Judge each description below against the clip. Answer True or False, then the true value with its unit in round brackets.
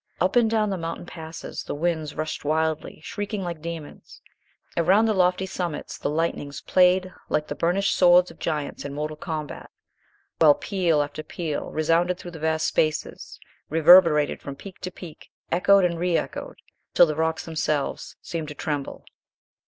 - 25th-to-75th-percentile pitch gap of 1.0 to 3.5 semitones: True (2.8 semitones)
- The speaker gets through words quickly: False (165 wpm)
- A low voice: False (165 Hz)